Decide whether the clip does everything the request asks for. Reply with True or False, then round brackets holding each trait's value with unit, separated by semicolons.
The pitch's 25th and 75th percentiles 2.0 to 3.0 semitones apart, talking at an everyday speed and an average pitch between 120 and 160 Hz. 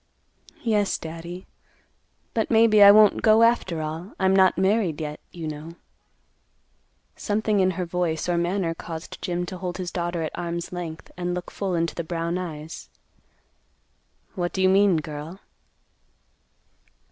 False (2.6 semitones; 145 wpm; 175 Hz)